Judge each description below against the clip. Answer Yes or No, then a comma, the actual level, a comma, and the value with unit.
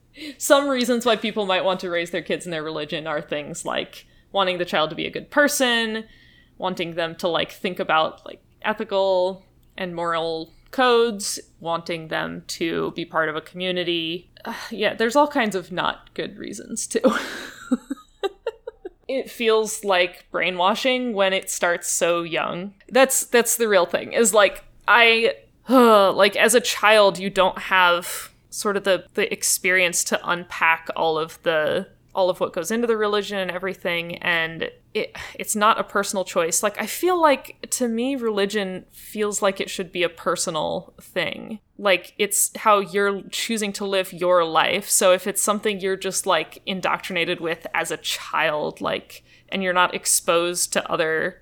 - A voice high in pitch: Yes, high, 195 Hz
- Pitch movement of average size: Yes, average, 4.1 semitones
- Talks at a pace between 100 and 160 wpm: No, average, 170 wpm